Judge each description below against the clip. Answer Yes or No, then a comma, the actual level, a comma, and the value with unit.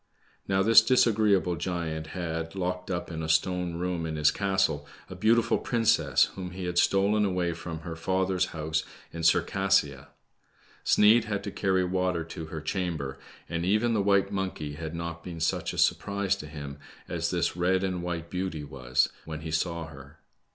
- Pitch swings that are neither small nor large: Yes, average, 3.1 semitones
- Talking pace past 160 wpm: Yes, average, 175 wpm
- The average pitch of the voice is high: No, very low, 90 Hz